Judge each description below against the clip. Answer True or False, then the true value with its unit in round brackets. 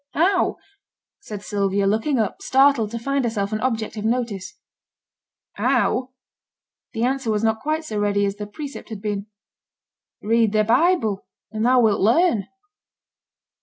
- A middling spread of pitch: True (3.8 semitones)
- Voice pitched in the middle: False (220 Hz)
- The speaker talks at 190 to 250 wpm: False (145 wpm)